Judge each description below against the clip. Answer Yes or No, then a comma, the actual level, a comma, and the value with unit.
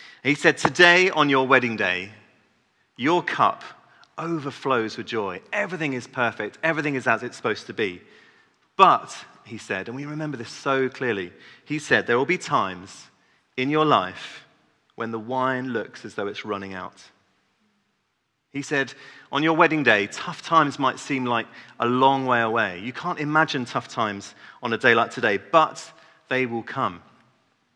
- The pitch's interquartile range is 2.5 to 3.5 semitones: No, average, 4.5 semitones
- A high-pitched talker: No, low, 135 Hz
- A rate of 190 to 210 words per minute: No, average, 170 wpm